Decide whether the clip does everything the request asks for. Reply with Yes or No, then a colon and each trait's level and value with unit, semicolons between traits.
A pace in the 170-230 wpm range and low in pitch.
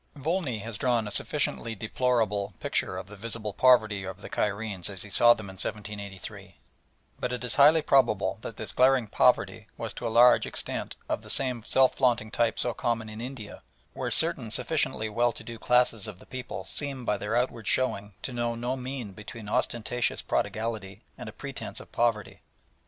Yes: average, 185 wpm; low, 115 Hz